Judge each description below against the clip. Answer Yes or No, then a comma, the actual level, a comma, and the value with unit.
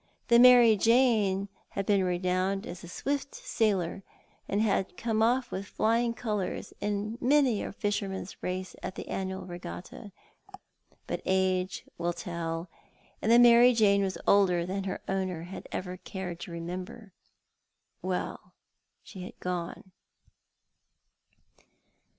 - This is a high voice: Yes, high, 195 Hz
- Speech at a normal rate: No, slow, 130 wpm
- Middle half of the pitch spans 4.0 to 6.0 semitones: No, average, 3.5 semitones